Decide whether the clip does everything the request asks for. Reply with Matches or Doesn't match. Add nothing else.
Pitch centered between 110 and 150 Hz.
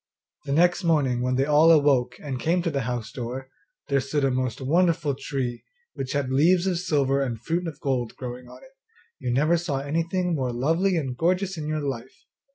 Matches